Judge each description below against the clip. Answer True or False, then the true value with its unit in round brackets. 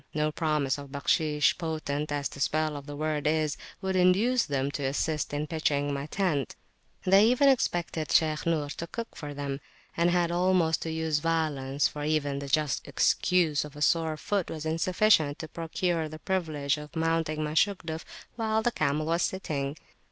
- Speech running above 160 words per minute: True (185 wpm)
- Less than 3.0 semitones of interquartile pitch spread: True (2.6 semitones)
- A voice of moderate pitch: True (155 Hz)